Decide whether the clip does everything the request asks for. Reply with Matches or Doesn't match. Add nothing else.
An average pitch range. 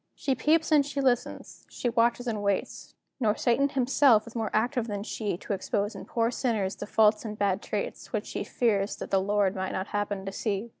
Matches